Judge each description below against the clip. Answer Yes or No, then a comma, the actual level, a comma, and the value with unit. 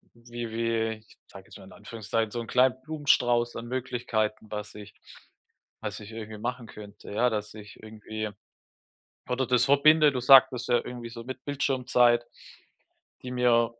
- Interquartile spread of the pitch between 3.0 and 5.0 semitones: No, narrow, 2.4 semitones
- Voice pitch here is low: Yes, low, 120 Hz